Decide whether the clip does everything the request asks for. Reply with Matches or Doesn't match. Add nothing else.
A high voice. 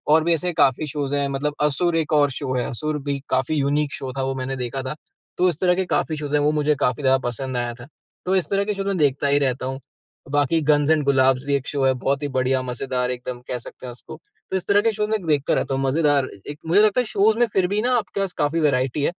Doesn't match